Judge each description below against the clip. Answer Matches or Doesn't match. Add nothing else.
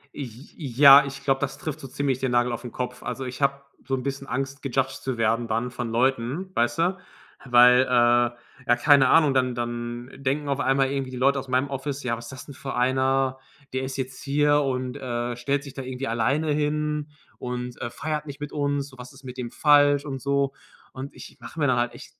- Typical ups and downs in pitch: Doesn't match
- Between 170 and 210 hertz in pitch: Doesn't match